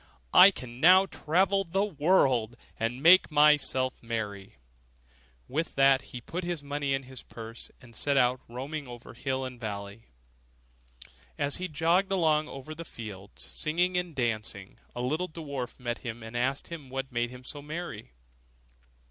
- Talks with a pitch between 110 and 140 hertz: Yes, low, 135 Hz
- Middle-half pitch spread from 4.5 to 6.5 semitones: Yes, average, 5.2 semitones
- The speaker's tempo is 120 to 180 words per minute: Yes, average, 165 wpm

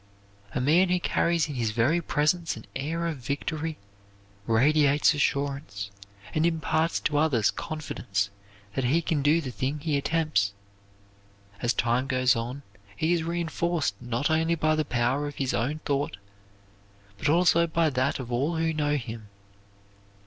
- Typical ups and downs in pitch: Yes, average, 4.2 semitones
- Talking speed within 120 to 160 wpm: Yes, average, 155 wpm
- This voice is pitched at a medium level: Yes, medium, 145 Hz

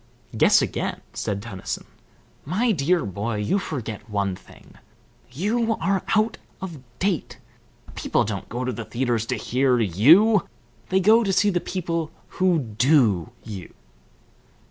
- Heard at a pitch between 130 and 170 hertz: Yes, low, 135 Hz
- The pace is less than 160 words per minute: Yes, average, 140 wpm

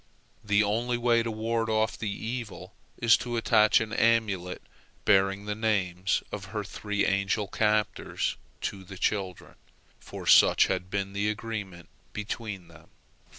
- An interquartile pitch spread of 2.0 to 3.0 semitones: Yes, narrow, 2.4 semitones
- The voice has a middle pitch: No, low, 105 Hz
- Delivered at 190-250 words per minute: No, average, 145 wpm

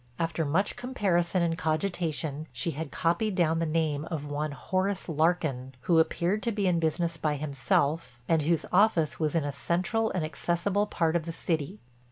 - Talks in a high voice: No, medium, 165 Hz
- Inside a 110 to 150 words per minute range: No, average, 180 wpm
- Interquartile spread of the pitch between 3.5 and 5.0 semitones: No, narrow, 2.6 semitones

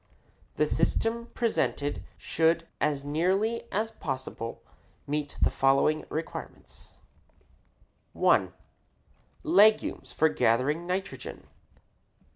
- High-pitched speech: No, medium, 160 Hz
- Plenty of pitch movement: Yes, wide, 6.9 semitones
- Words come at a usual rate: No, slow, 85 wpm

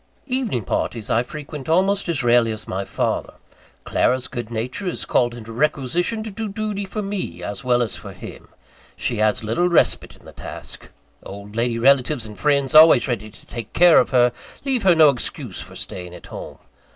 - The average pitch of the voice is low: Yes, low, 130 Hz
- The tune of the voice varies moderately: No, wide, 7.5 semitones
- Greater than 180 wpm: Yes, average, 190 wpm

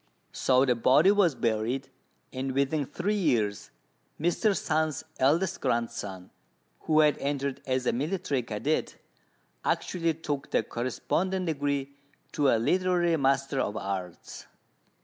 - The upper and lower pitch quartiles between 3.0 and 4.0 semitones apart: No, average, 4.4 semitones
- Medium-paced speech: No, slow, 125 wpm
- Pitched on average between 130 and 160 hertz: Yes, medium, 140 Hz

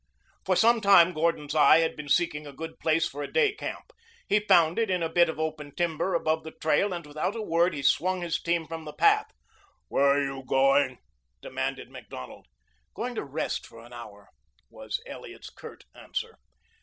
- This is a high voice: No, medium, 160 Hz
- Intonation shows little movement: No, average, 3.8 semitones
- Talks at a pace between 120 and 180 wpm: No, average, 195 wpm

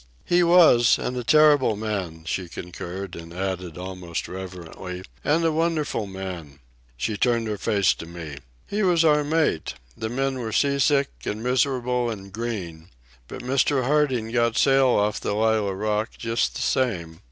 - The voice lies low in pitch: Yes, low, 110 Hz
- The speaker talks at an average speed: Yes, average, 165 wpm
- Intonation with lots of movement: Yes, wide, 6.4 semitones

